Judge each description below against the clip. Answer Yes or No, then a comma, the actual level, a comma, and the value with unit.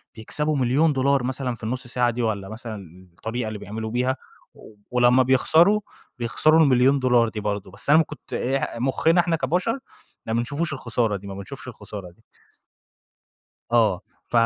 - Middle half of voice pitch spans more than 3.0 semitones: Yes, average, 4.0 semitones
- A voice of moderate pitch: No, low, 125 Hz